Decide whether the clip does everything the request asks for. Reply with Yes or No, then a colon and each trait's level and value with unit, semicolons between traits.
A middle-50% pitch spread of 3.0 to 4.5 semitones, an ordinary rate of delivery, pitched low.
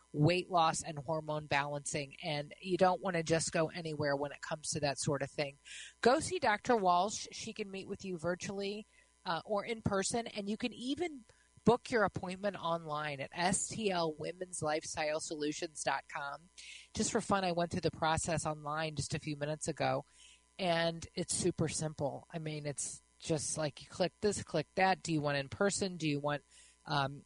No: average, 3.9 semitones; average, 185 wpm; medium, 165 Hz